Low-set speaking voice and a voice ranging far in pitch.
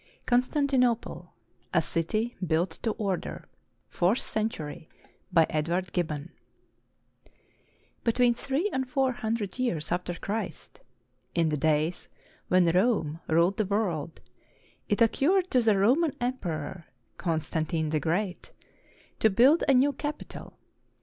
No: high, 195 Hz; wide, 6.8 semitones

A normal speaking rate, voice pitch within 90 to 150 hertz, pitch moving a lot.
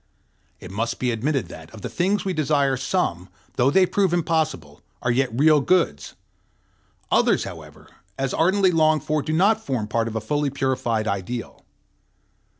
Yes: average, 160 wpm; low, 135 Hz; wide, 5.9 semitones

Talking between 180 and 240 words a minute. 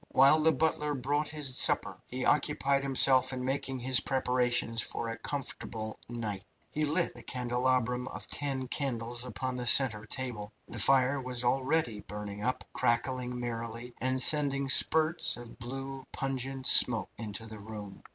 No: average, 150 wpm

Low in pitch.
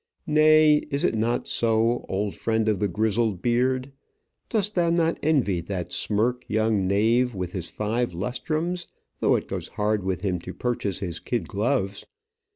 Yes: low, 110 Hz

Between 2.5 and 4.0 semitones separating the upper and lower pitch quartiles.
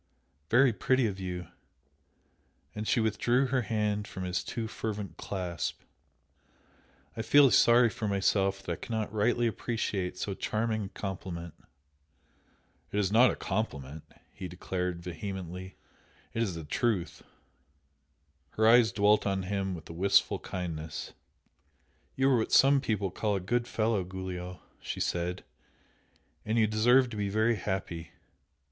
Yes: average, 3.7 semitones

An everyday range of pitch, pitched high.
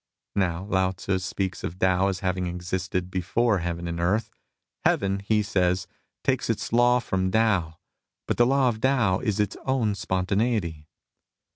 No: average, 3.2 semitones; very low, 95 Hz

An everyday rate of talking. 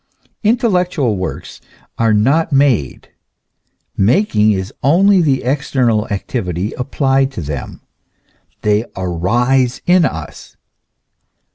No: slow, 95 wpm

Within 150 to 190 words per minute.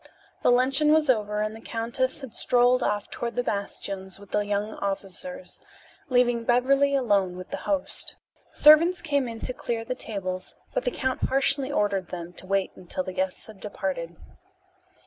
Yes: average, 170 wpm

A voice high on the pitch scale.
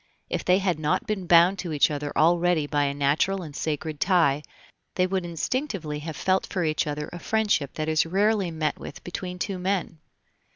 No: medium, 170 Hz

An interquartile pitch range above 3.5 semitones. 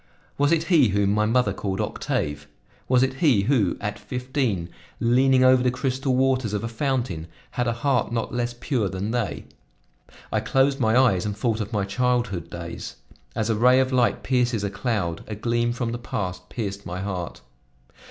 Yes: average, 4.2 semitones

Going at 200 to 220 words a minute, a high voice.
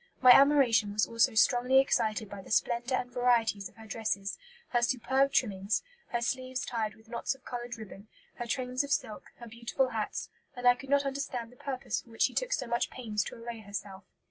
Yes: fast, 205 wpm; high, 240 Hz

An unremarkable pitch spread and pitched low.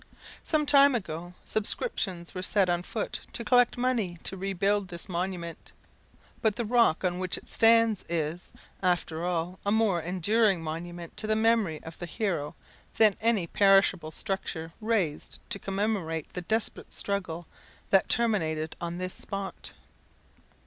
No: average, 4.1 semitones; high, 190 Hz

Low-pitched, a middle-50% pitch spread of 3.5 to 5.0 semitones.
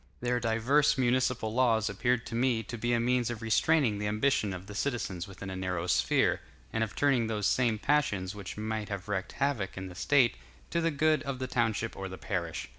Yes: low, 115 Hz; average, 4.1 semitones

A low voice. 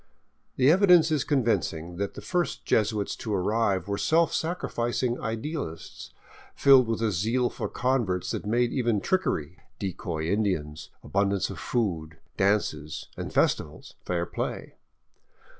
Yes: low, 110 Hz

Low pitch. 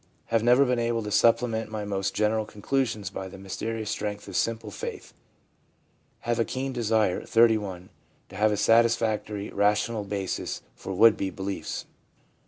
Yes: low, 110 Hz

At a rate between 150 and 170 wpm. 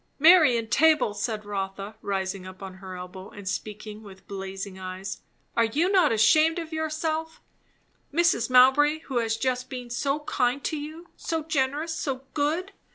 Yes: average, 160 wpm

